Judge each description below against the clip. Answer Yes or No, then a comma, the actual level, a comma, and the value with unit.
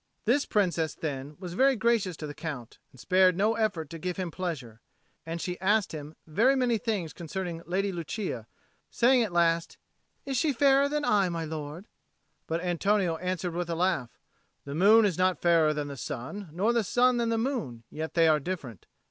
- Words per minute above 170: Yes, average, 195 wpm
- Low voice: No, medium, 180 Hz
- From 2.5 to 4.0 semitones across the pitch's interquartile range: No, average, 5.2 semitones